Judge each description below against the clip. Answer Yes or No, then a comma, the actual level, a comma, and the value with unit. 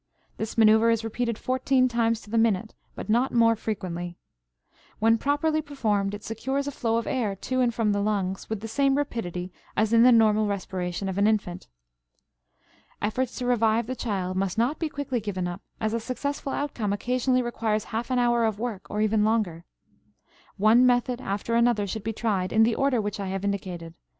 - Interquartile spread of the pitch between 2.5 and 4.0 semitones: Yes, average, 3.2 semitones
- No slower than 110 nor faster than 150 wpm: No, average, 195 wpm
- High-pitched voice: Yes, high, 225 Hz